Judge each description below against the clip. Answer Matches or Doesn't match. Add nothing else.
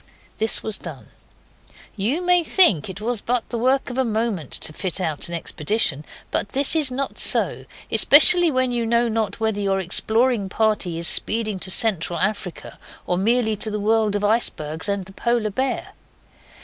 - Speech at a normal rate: Matches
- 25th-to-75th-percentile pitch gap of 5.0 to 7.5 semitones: Doesn't match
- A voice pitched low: Doesn't match